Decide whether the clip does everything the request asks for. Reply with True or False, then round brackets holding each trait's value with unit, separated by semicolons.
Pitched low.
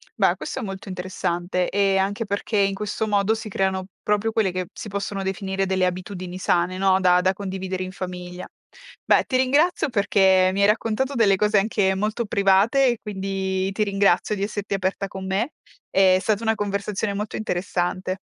False (195 Hz)